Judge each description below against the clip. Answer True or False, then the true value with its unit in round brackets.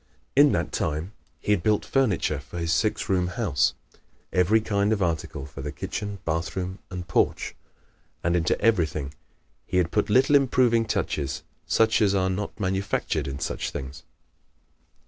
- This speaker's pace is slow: False (155 wpm)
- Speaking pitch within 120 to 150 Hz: False (95 Hz)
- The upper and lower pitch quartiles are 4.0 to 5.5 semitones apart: True (4.6 semitones)